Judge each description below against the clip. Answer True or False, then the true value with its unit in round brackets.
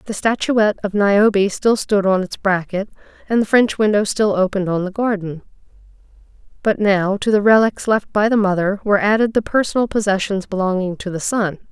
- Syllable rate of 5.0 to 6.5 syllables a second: True (5.5 syllables/s)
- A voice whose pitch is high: True (200 Hz)